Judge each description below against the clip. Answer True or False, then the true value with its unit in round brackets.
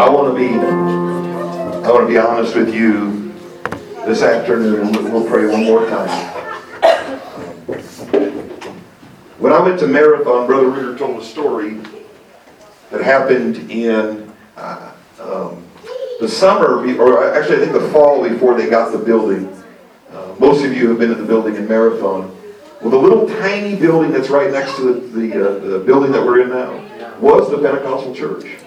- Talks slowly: False (175 wpm)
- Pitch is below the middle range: True (120 Hz)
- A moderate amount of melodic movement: True (4.7 semitones)